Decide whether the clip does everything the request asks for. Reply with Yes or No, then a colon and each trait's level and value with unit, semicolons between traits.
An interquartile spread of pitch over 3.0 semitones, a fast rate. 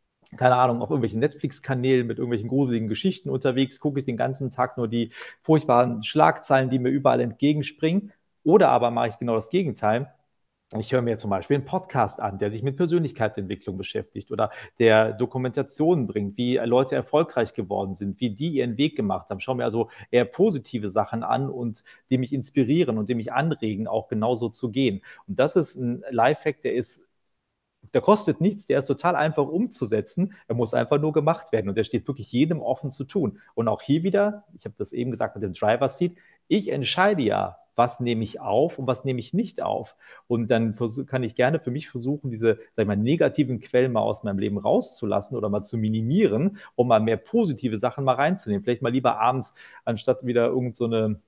Yes: average, 4.1 semitones; fast, 200 wpm